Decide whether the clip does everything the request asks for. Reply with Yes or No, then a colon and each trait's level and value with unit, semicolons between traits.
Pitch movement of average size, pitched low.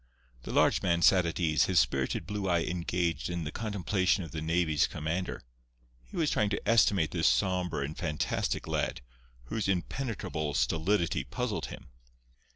Yes: average, 3.5 semitones; very low, 85 Hz